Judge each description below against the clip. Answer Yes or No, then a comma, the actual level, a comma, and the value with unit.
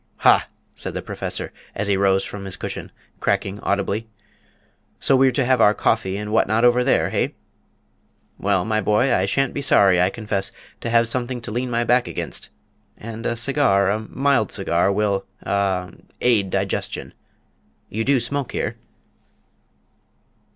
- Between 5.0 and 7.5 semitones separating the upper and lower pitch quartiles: No, average, 3.7 semitones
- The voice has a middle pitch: No, low, 110 Hz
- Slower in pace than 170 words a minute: Yes, average, 160 wpm